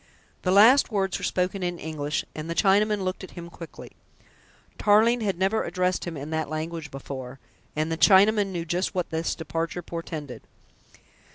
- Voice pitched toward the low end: No, medium, 175 Hz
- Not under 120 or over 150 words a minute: No, average, 170 wpm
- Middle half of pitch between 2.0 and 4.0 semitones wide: Yes, average, 3.5 semitones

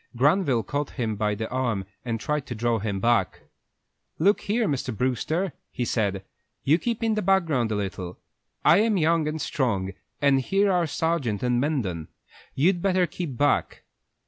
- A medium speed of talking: Yes, average, 170 wpm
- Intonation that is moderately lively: No, wide, 7.2 semitones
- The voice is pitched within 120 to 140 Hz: Yes, low, 135 Hz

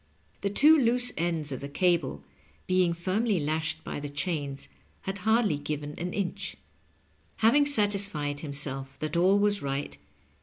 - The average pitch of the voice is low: No, medium, 170 Hz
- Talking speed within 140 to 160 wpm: Yes, average, 145 wpm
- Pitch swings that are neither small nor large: No, wide, 5.8 semitones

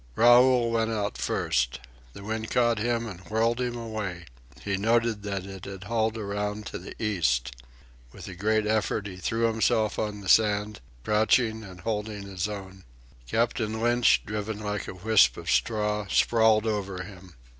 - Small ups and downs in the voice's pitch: Yes, narrow, 2.2 semitones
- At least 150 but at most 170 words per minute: Yes, average, 165 wpm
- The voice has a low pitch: Yes, low, 105 Hz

